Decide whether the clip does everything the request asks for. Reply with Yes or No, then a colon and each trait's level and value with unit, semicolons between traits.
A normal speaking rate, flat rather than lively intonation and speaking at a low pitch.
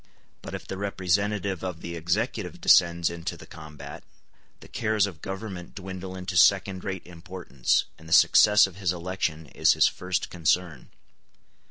Yes: average, 155 wpm; narrow, 2.2 semitones; very low, 90 Hz